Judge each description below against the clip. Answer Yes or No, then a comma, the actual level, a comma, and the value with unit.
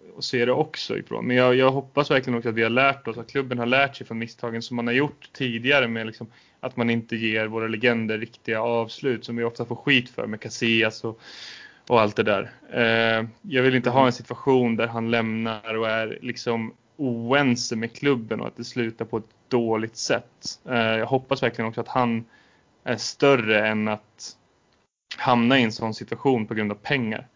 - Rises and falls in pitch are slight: Yes, narrow, 1.9 semitones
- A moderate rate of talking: No, fast, 200 wpm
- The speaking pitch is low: Yes, low, 115 Hz